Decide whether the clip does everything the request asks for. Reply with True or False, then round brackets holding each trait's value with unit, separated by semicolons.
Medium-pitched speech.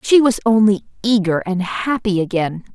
False (205 Hz)